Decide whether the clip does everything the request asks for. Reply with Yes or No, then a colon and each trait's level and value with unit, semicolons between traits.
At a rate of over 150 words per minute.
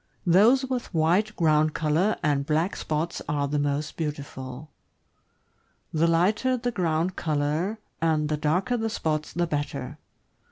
No: slow, 135 wpm